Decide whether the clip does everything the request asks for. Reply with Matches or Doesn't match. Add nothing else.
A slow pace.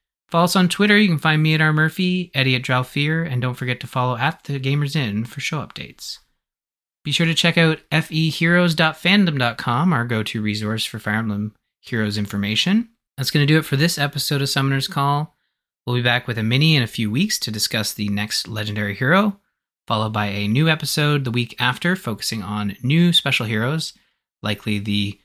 Doesn't match